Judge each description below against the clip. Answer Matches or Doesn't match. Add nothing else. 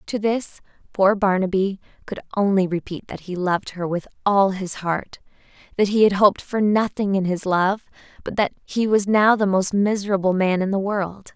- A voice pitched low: Doesn't match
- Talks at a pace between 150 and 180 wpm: Doesn't match